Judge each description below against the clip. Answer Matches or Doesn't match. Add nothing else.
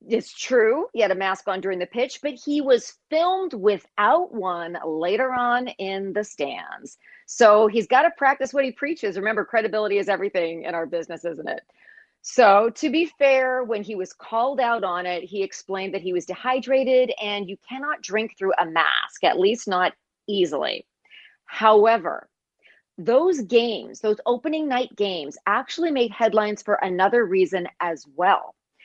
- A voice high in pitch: Matches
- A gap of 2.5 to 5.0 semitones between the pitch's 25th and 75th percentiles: Doesn't match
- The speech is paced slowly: Doesn't match